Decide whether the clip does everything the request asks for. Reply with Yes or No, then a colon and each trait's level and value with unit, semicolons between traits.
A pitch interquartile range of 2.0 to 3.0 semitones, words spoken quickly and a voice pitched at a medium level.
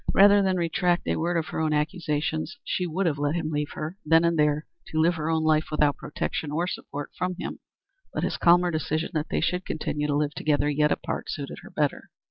Yes: narrow, 2.5 semitones; fast, 225 wpm; medium, 155 Hz